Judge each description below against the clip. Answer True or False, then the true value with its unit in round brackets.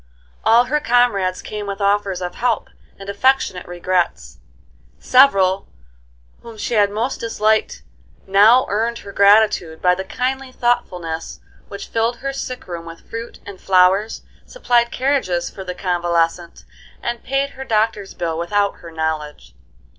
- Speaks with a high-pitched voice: True (200 Hz)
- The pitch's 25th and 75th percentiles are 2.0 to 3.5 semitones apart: False (4.9 semitones)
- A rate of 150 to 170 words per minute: False (140 wpm)